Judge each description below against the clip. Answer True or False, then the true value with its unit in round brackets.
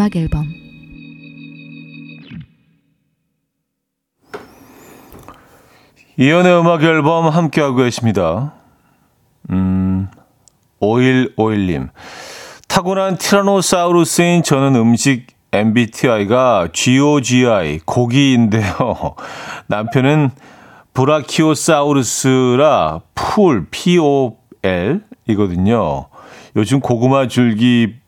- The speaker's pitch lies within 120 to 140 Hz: True (135 Hz)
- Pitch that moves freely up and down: False (5.0 semitones)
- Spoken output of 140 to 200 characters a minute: True (170 characters per minute)